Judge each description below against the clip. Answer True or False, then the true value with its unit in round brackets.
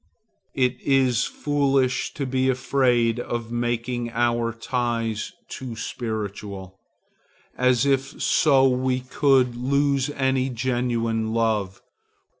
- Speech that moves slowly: True (100 wpm)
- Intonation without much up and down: True (2.3 semitones)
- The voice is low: True (125 Hz)